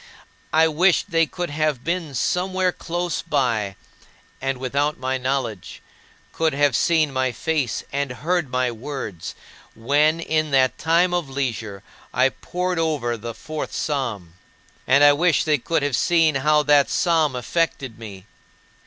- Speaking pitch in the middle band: Yes, medium, 145 Hz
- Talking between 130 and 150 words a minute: Yes, average, 145 wpm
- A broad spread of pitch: No, average, 4.2 semitones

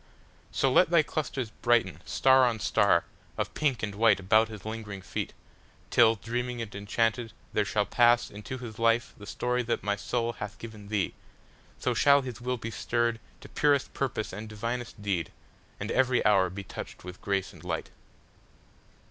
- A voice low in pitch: Yes, low, 115 Hz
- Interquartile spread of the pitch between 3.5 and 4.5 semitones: No, average, 3.0 semitones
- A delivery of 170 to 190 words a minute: No, average, 155 wpm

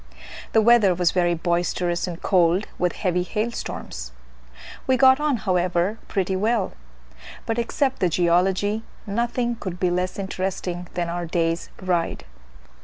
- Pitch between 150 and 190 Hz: Yes, medium, 185 Hz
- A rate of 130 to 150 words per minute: Yes, average, 140 wpm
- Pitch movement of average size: Yes, average, 3.9 semitones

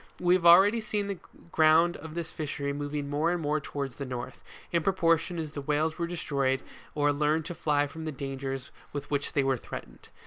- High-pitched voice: No, medium, 150 Hz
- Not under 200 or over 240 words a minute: Yes, fast, 205 wpm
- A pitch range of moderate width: Yes, average, 3.0 semitones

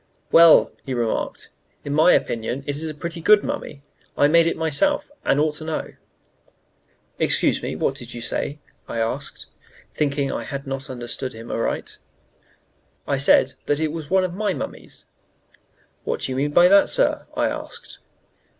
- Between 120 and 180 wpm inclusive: Yes, average, 170 wpm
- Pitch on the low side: No, medium, 145 Hz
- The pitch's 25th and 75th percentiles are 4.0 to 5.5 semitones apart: No, average, 3.6 semitones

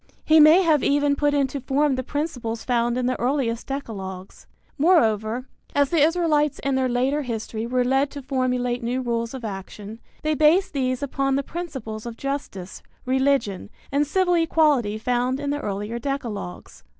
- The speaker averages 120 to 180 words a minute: Yes, average, 165 wpm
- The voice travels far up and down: No, average, 3.8 semitones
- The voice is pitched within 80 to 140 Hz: No, very high, 265 Hz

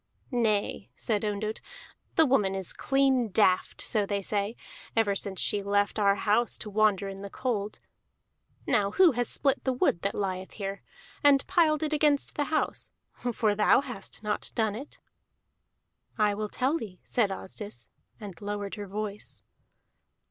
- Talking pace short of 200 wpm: Yes, average, 155 wpm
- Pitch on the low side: No, high, 210 Hz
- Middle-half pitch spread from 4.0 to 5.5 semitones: No, average, 3.5 semitones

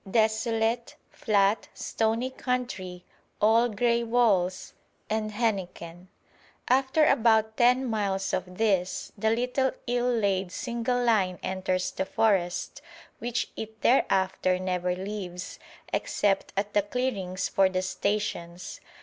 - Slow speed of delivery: Yes, slow, 115 wpm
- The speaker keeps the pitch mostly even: No, average, 4.0 semitones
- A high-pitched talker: Yes, high, 210 Hz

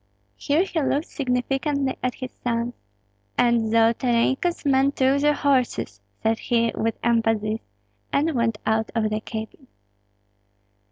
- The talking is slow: Yes, slow, 125 wpm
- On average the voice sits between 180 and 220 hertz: No, high, 245 Hz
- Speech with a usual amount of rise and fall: Yes, average, 3.5 semitones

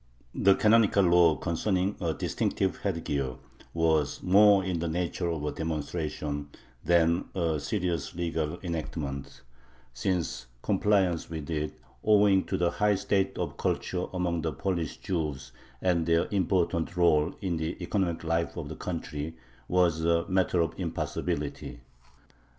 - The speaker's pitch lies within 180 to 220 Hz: No, very low, 85 Hz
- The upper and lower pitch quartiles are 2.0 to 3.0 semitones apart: Yes, narrow, 2.6 semitones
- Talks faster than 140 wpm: No, slow, 135 wpm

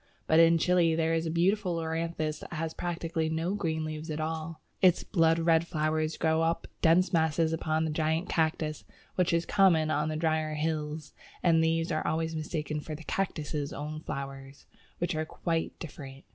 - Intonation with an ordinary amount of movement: No, narrow, 1.1 semitones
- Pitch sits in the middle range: Yes, medium, 160 Hz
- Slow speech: No, average, 180 wpm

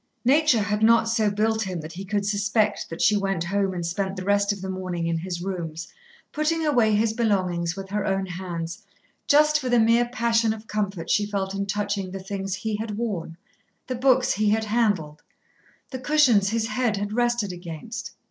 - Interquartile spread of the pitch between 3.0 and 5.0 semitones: Yes, average, 3.3 semitones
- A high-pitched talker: Yes, high, 205 Hz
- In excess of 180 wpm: Yes, average, 195 wpm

